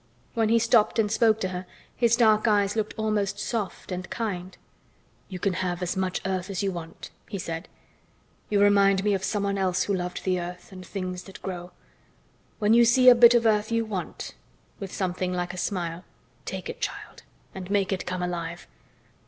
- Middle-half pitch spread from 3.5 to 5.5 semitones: No, average, 2.9 semitones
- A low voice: No, high, 195 Hz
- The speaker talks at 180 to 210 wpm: Yes, average, 195 wpm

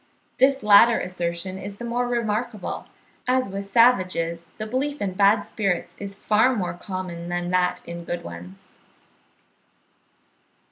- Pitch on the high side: Yes, high, 200 Hz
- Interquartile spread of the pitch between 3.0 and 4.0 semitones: No, average, 4.9 semitones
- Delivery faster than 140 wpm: No, slow, 135 wpm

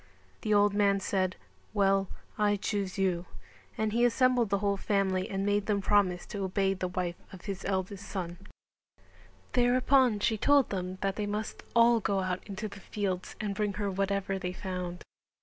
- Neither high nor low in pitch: No, high, 200 Hz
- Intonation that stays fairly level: Yes, narrow, 1.8 semitones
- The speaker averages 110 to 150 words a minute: No, average, 175 wpm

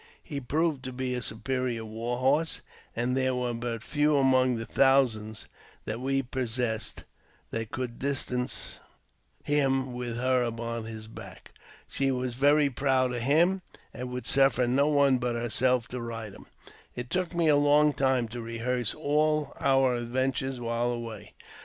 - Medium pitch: No, low, 125 Hz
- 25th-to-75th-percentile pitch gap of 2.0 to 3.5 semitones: Yes, narrow, 2.5 semitones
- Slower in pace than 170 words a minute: Yes, average, 160 wpm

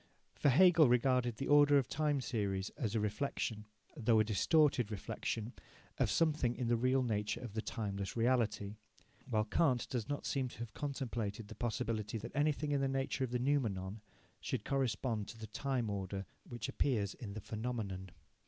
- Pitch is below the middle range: Yes, low, 120 Hz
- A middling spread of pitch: Yes, average, 4.1 semitones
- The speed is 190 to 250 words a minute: No, average, 180 wpm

